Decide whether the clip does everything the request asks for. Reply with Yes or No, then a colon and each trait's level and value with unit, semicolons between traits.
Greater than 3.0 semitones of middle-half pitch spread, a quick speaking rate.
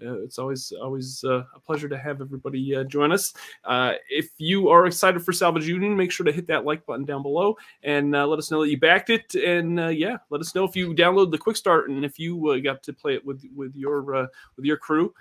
Yes: average, 4.2 semitones; fast, 260 wpm